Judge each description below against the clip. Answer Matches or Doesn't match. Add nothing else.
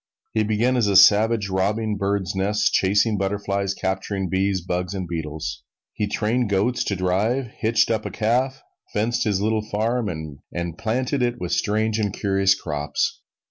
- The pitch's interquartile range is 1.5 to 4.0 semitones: Matches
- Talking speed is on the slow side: Doesn't match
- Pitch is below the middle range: Matches